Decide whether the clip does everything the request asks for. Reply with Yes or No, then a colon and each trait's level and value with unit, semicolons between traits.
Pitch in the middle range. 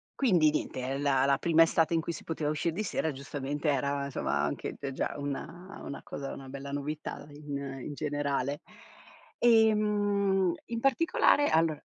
Yes: medium, 150 Hz